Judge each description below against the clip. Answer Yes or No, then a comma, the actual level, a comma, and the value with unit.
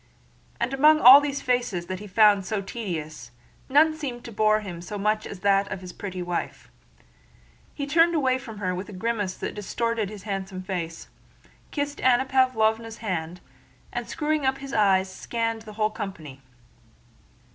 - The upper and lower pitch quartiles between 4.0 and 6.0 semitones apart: Yes, average, 5.2 semitones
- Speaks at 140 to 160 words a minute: No, average, 170 wpm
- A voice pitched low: No, high, 215 Hz